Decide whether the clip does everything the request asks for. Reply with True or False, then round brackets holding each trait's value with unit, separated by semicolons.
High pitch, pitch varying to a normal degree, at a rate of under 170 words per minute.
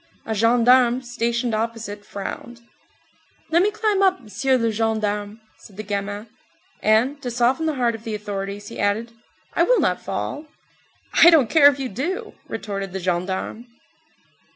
True (230 Hz; 4.1 semitones; 155 wpm)